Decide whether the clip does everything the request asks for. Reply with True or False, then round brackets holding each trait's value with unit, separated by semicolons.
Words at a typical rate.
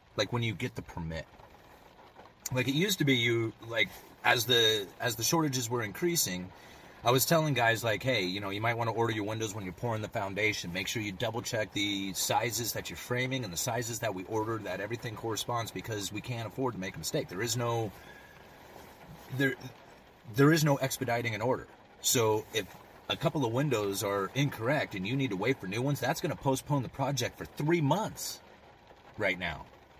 False (210 wpm)